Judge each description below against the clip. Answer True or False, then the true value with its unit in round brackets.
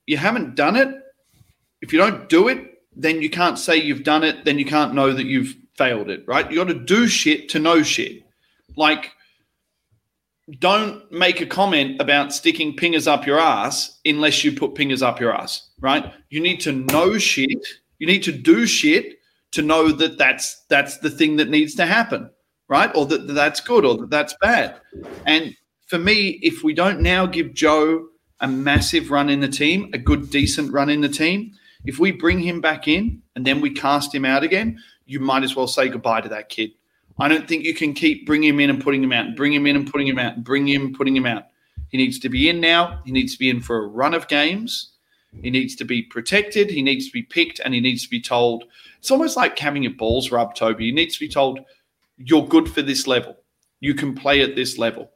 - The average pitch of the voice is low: False (150 Hz)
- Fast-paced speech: True (230 wpm)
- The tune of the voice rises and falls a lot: True (6.0 semitones)